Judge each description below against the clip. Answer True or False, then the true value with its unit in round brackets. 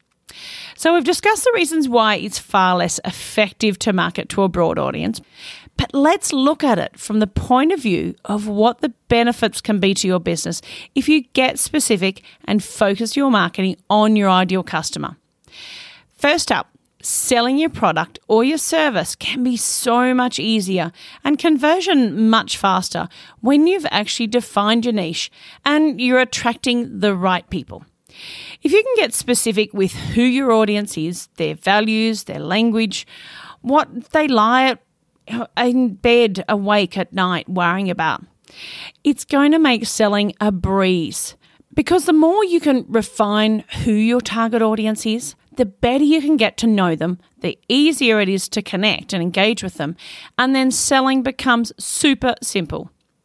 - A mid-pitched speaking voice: False (225 Hz)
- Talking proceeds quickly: False (160 wpm)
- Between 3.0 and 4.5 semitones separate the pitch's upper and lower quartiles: False (5.3 semitones)